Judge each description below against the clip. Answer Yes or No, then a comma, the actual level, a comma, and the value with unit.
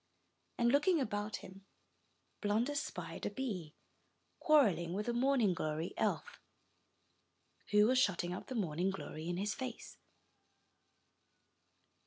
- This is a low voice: No, high, 210 Hz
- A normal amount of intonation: No, wide, 6.2 semitones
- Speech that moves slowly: Yes, slow, 120 wpm